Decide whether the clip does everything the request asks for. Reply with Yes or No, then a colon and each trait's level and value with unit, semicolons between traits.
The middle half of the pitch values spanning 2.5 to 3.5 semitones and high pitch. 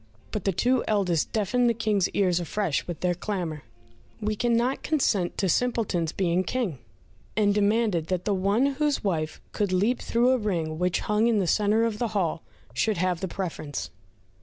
No: average, 4.4 semitones; high, 200 Hz